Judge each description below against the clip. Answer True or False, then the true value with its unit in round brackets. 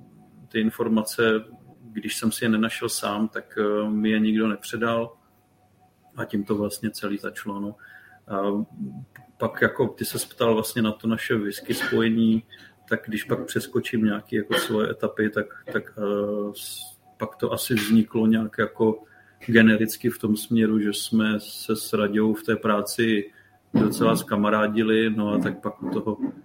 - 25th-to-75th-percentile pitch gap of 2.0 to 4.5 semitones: False (1.3 semitones)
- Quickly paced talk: False (155 wpm)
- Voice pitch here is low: True (110 Hz)